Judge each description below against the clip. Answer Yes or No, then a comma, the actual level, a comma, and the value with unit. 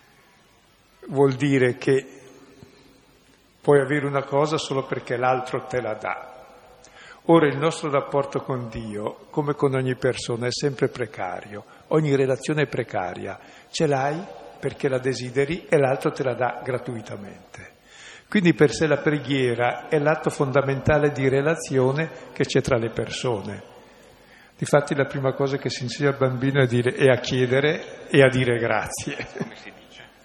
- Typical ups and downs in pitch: No, narrow, 2.2 semitones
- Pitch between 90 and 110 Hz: No, low, 135 Hz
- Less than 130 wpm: No, average, 150 wpm